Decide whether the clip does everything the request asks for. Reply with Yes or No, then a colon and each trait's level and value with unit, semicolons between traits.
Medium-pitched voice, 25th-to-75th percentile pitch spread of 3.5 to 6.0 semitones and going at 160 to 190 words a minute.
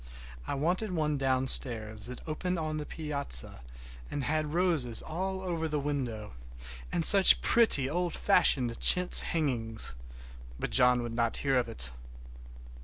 No: medium, 145 Hz; average, 5.2 semitones; average, 140 wpm